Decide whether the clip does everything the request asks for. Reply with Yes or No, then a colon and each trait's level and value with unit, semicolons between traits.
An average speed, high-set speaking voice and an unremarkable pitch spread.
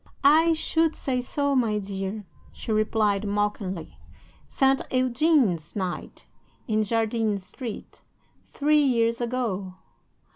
No: slow, 105 wpm; high, 225 Hz; average, 4.7 semitones